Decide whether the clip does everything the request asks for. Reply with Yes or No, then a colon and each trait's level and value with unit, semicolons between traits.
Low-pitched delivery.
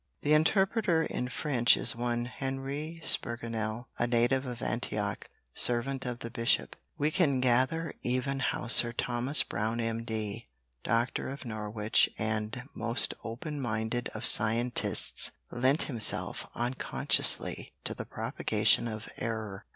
Yes: low, 120 Hz